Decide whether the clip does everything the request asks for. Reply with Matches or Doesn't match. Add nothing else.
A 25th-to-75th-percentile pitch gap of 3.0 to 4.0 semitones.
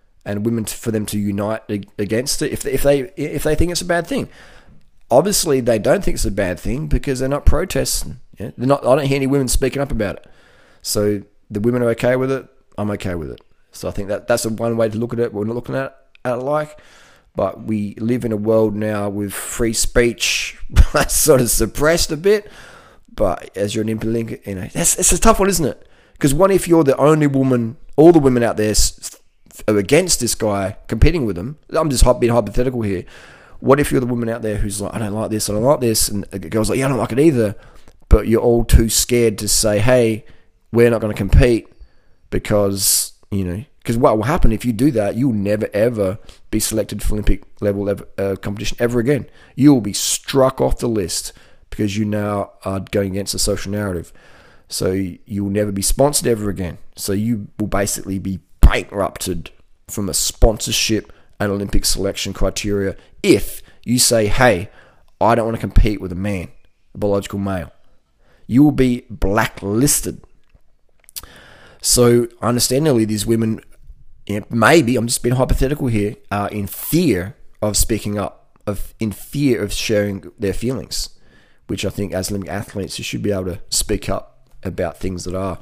Matches